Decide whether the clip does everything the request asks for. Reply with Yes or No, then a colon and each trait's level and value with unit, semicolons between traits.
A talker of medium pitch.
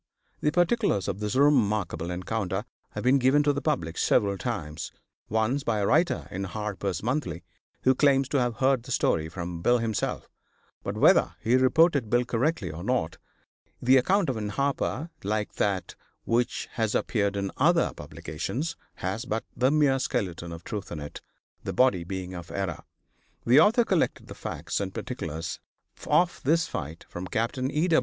No: low, 115 Hz